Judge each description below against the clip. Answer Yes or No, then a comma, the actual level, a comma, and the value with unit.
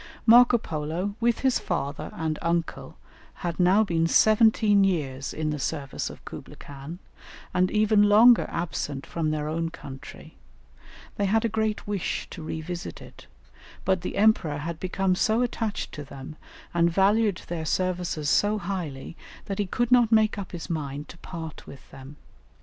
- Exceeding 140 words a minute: Yes, average, 165 wpm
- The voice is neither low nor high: Yes, medium, 175 Hz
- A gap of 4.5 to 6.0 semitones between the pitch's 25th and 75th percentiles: Yes, average, 5.1 semitones